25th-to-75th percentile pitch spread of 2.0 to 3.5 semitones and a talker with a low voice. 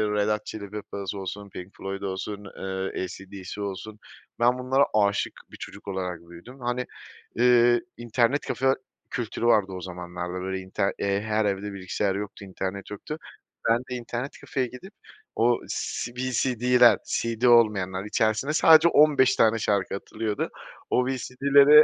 No: average, 4.2 semitones; low, 105 Hz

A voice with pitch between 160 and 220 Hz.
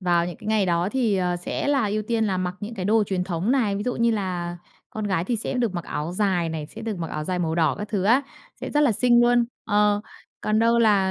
Yes: high, 205 Hz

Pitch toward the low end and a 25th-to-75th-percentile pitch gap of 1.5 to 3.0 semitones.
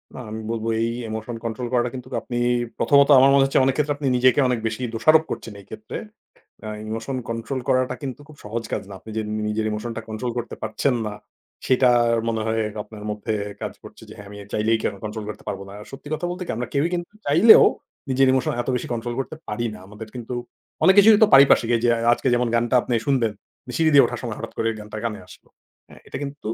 No: low, 120 Hz; average, 3.6 semitones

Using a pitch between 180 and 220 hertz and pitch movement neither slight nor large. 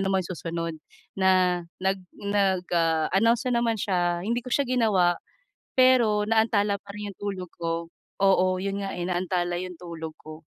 Yes: high, 190 Hz; average, 3.0 semitones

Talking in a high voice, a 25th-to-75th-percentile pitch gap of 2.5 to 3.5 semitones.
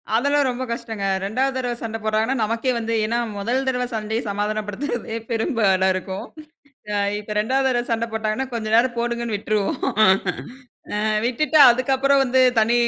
Yes: high, 235 Hz; average, 3.1 semitones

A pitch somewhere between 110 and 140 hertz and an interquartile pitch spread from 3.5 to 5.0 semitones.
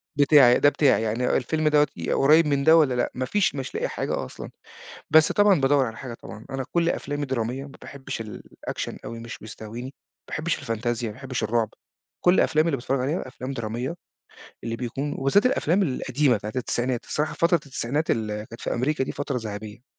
Yes: low, 135 Hz; average, 4.1 semitones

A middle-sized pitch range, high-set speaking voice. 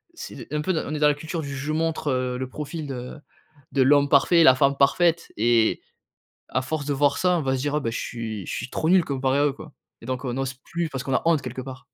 No: average, 3.0 semitones; medium, 140 Hz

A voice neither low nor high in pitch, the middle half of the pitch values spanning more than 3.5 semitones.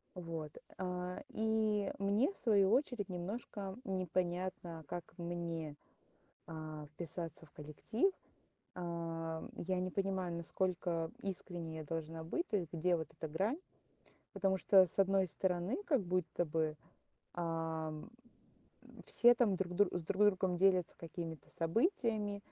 No: medium, 180 Hz; average, 3.2 semitones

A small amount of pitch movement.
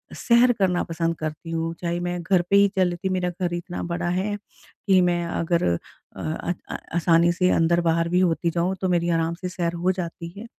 Yes: narrow, 1.5 semitones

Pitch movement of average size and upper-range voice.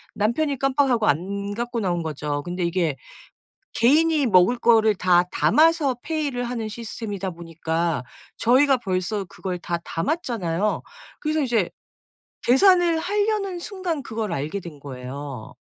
No: wide, 8.3 semitones; high, 220 Hz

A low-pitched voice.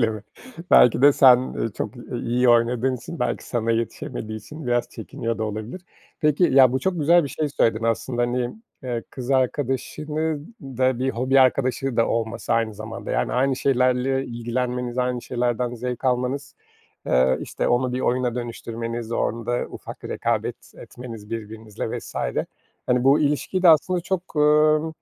Yes: low, 125 Hz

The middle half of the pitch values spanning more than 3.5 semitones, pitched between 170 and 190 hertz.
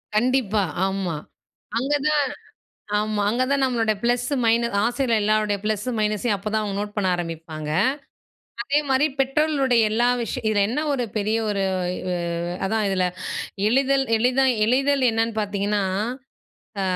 No: average, 3.9 semitones; high, 225 Hz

